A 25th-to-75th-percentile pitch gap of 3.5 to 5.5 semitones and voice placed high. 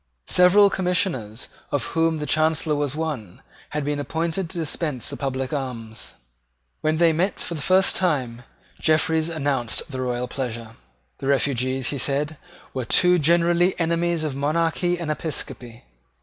No: average, 4.2 semitones; medium, 150 Hz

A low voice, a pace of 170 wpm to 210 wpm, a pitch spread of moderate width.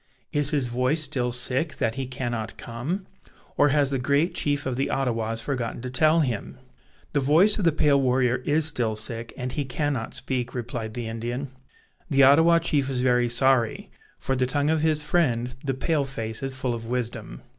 Yes: low, 130 Hz; average, 190 wpm; average, 3.2 semitones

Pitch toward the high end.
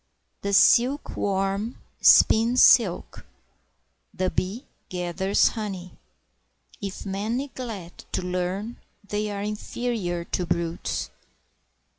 Yes: high, 200 Hz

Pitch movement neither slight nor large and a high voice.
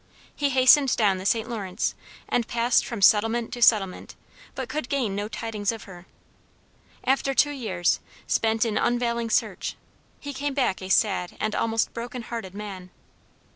Yes: average, 3.3 semitones; high, 225 Hz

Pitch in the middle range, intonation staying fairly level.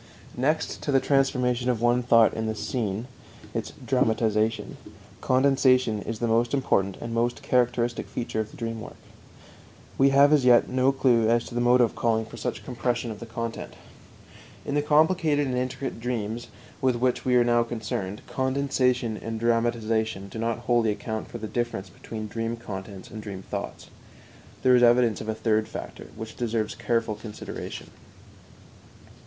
No: low, 120 Hz; narrow, 2.3 semitones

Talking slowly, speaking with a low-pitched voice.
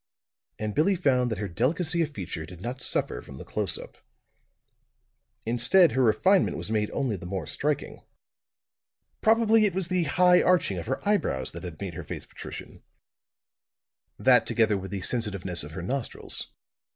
No: average, 165 wpm; low, 120 Hz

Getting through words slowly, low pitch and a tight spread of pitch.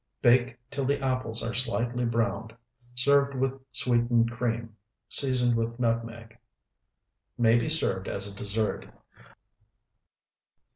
Yes: slow, 110 wpm; low, 120 Hz; narrow, 1.9 semitones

